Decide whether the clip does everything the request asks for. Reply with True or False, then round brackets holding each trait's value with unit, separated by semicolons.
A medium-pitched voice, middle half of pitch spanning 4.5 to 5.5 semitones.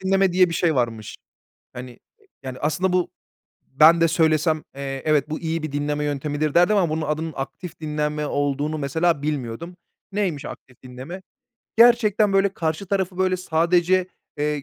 False (155 Hz; 3.7 semitones)